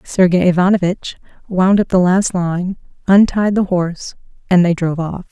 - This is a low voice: No, medium, 185 Hz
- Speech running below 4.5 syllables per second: No, 5.0 syllables/s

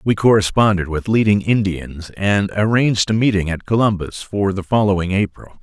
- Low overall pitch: Yes, low, 100 Hz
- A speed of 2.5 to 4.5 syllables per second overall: No, 5.1 syllables/s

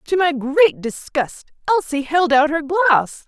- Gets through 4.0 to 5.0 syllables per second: No, 3.7 syllables/s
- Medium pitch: No, very high, 310 Hz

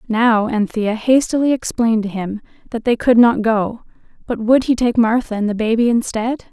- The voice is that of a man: No, female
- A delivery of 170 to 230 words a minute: Yes, average, 185 wpm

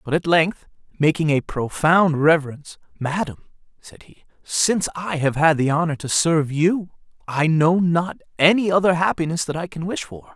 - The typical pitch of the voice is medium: Yes, medium, 160 Hz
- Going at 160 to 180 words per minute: Yes, average, 175 wpm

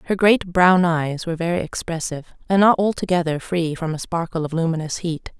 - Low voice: No, medium, 170 Hz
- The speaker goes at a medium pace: Yes, average, 190 wpm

